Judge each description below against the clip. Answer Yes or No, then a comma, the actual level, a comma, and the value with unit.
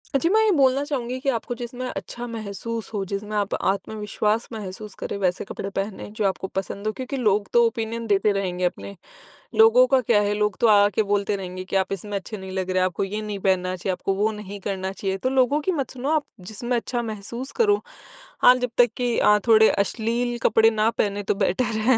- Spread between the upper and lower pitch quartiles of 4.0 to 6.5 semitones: No, average, 3.6 semitones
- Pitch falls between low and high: No, high, 215 Hz